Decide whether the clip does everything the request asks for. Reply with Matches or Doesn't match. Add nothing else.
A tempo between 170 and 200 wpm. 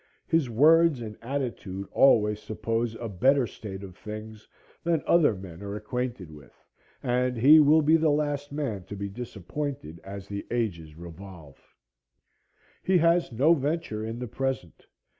Doesn't match